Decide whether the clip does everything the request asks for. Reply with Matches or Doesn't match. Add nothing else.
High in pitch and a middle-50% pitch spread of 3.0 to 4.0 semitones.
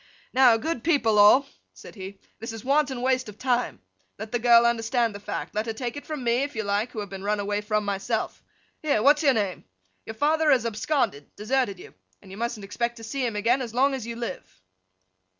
Matches